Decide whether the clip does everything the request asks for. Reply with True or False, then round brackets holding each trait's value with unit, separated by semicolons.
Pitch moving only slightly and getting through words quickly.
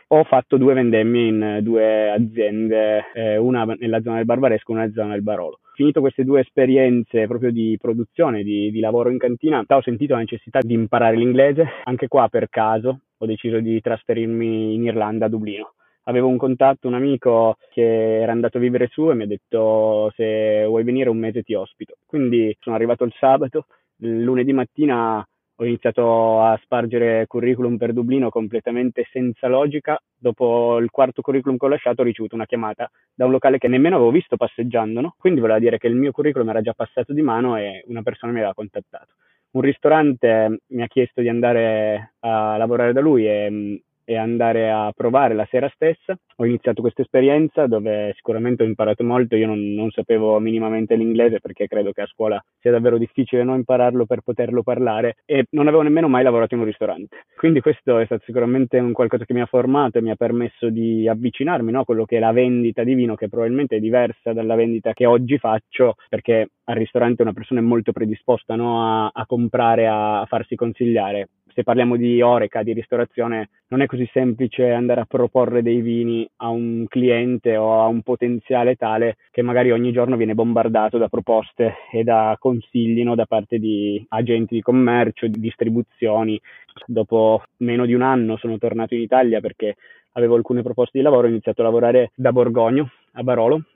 True (1.9 semitones; 195 wpm)